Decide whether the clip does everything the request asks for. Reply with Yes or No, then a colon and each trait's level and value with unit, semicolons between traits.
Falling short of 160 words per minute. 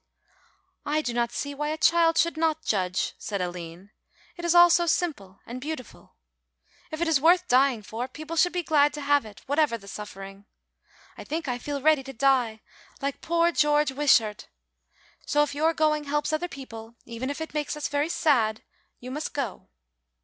No: average, 185 wpm